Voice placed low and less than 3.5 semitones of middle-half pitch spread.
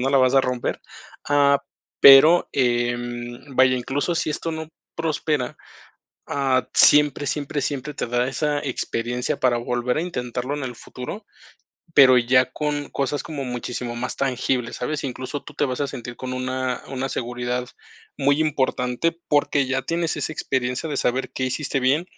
Yes: low, 130 Hz; average, 2.7 semitones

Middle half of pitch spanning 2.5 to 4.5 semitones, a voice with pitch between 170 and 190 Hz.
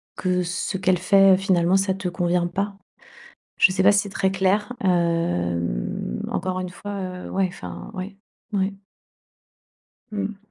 No: narrow, 1.8 semitones; medium, 185 Hz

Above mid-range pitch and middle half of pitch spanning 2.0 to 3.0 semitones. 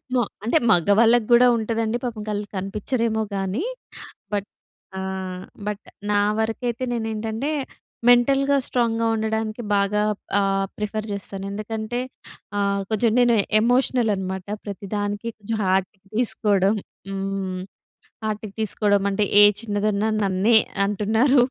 Yes: high, 215 Hz; narrow, 2.4 semitones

